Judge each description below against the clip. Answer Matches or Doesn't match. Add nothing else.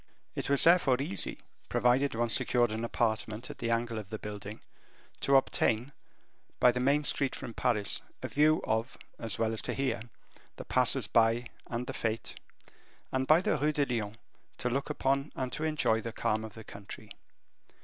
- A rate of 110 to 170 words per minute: Doesn't match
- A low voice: Matches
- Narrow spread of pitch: Doesn't match